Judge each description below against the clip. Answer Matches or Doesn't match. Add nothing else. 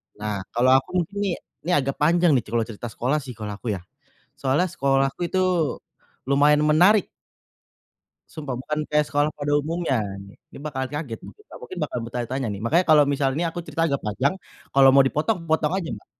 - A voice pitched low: Doesn't match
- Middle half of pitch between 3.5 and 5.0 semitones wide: Matches